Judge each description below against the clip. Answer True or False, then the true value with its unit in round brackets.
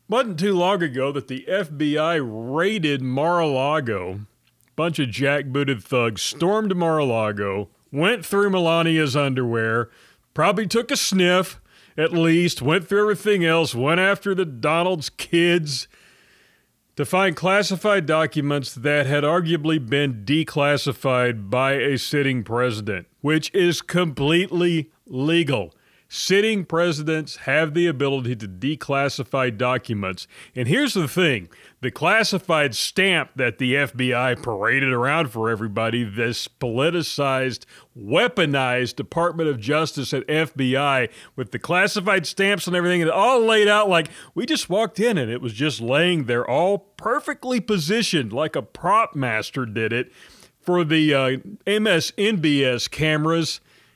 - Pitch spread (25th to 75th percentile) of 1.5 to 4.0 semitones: False (5.5 semitones)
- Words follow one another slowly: True (130 wpm)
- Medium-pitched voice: True (150 Hz)